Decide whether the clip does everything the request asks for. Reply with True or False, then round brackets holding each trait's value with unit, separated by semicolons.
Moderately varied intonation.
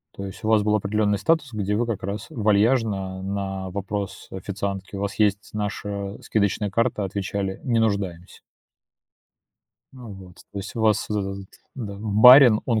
False (1.8 semitones)